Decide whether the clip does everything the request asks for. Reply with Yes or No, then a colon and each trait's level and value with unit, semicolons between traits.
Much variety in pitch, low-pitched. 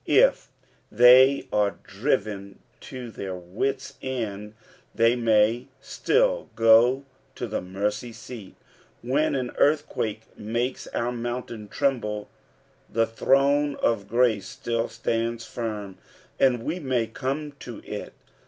No: average, 3.5 semitones; low, 115 Hz